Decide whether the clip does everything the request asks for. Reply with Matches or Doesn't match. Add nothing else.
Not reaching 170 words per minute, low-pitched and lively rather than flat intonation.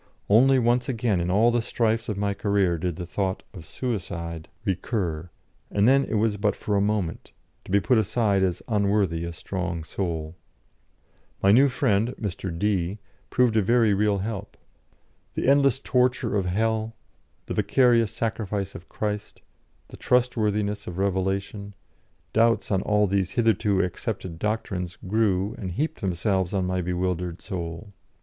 Doesn't match